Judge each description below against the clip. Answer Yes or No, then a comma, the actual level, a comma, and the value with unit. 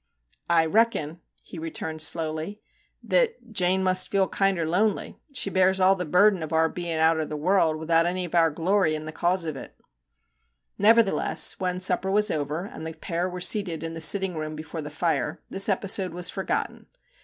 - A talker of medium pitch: Yes, medium, 175 Hz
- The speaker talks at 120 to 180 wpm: No, average, 195 wpm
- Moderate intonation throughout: Yes, average, 3.1 semitones